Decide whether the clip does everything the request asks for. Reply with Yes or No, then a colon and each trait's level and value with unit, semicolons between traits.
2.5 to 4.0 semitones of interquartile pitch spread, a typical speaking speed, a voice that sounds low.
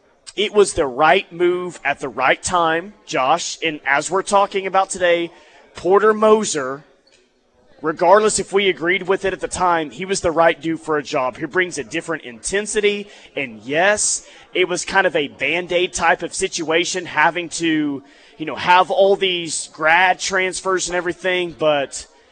No: average, 3.4 semitones; average, 170 wpm; medium, 175 Hz